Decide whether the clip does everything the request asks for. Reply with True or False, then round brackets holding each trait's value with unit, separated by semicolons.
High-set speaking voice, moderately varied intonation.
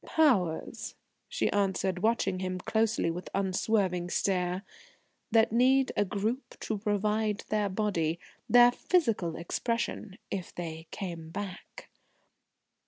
True (200 Hz; 3.7 semitones)